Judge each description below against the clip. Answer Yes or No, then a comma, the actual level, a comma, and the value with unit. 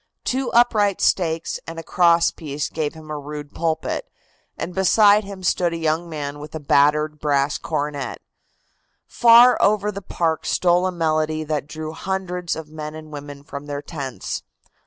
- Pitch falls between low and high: Yes, medium, 160 Hz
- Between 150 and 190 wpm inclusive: Yes, average, 165 wpm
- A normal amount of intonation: Yes, average, 3.5 semitones